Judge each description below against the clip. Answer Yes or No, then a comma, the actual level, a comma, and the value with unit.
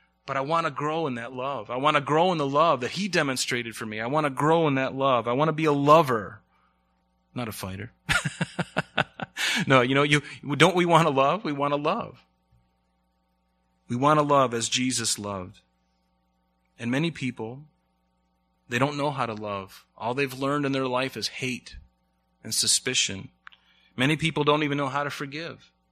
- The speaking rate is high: No, average, 190 wpm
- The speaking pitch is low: Yes, low, 125 Hz